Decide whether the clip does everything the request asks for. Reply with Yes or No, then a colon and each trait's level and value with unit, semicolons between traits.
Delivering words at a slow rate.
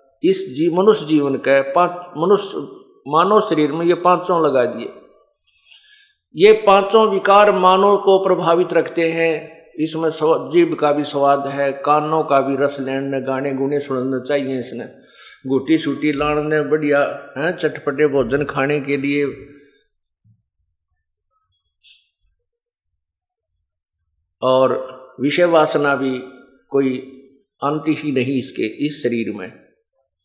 No: average, 120 wpm